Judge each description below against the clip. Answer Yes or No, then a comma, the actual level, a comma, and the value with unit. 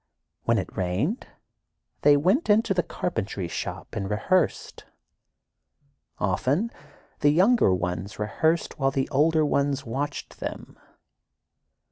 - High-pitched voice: No, medium, 140 Hz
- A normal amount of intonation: No, wide, 8.9 semitones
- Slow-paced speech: Yes, slow, 110 wpm